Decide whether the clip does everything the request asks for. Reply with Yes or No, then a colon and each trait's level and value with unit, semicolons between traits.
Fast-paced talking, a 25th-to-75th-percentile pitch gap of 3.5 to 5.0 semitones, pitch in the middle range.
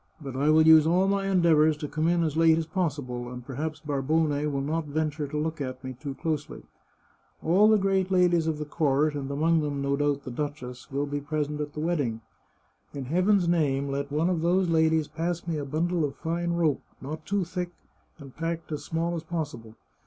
No: fast, 210 wpm; average, 2.9 semitones; medium, 155 Hz